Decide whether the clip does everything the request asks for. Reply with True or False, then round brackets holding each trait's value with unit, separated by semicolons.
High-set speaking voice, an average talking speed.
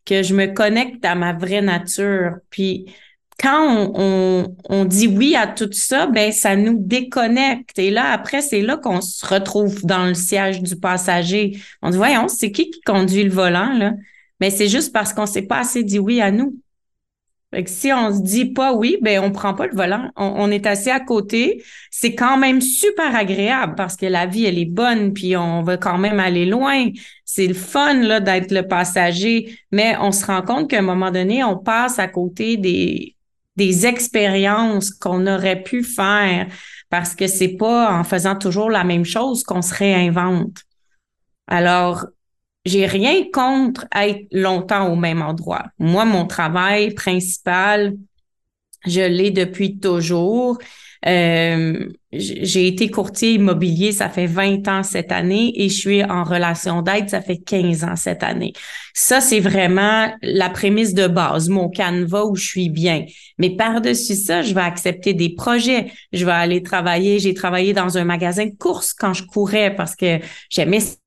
True (195 Hz; 180 wpm)